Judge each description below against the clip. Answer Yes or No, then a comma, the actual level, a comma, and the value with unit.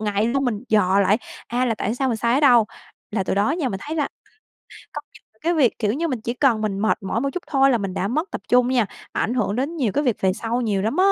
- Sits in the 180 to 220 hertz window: No, high, 235 Hz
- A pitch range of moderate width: Yes, average, 4.5 semitones